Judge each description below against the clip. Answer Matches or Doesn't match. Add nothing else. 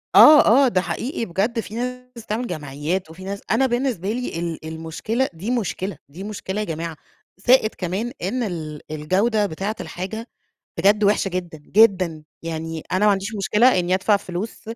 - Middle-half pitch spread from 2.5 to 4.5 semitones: Doesn't match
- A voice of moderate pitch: Doesn't match